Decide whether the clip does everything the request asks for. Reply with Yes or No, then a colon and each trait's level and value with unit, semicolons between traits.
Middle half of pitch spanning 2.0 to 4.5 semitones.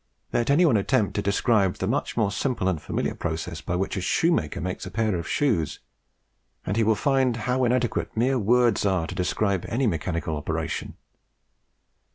No: wide, 5.4 semitones